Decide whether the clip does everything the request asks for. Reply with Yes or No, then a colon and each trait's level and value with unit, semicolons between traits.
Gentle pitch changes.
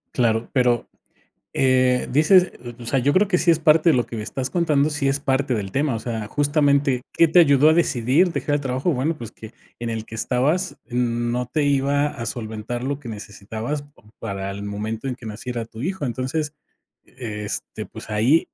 No: average, 4.2 semitones